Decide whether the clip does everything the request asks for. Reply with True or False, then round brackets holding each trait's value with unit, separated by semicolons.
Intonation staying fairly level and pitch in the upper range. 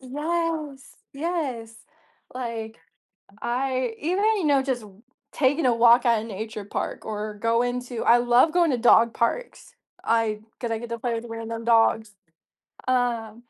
False (3.0 semitones; 240 Hz)